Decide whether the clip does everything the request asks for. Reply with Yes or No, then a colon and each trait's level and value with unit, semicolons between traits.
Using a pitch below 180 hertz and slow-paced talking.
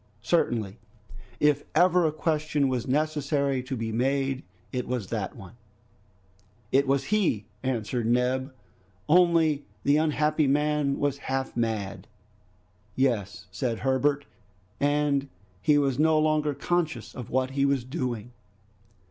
Yes: medium, 140 Hz; slow, 125 wpm